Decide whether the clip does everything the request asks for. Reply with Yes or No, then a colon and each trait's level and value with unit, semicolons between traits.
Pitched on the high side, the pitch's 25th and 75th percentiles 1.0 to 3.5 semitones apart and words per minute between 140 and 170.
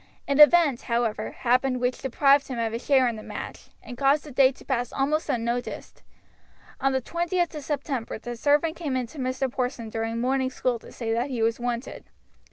No: very high, 255 Hz; average, 2.9 semitones; average, 200 wpm